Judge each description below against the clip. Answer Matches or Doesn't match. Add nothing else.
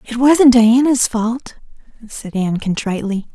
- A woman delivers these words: Matches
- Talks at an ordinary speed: Doesn't match